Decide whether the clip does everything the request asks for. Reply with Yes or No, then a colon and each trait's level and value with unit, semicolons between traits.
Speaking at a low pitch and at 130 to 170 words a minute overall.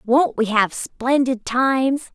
No: very high, 255 Hz; average, 140 wpm